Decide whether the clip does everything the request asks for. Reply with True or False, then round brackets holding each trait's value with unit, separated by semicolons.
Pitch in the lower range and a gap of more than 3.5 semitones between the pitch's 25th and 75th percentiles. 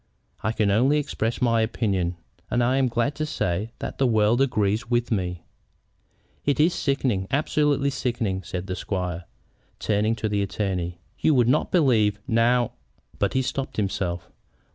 True (110 Hz; 4.9 semitones)